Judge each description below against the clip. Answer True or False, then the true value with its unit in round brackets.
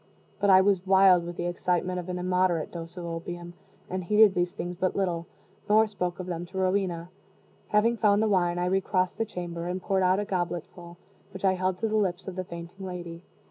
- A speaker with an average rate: False (215 wpm)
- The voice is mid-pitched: True (180 Hz)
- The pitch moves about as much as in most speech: False (1.7 semitones)